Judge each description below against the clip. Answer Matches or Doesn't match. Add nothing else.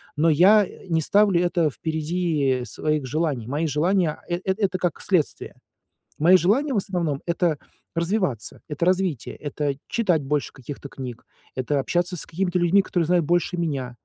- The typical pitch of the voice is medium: Matches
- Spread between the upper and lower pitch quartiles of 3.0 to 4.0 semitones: Matches